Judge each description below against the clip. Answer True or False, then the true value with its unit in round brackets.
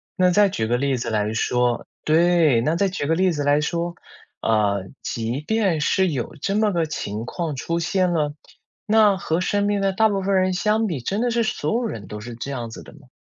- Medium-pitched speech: True (165 Hz)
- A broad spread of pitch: True (8.0 semitones)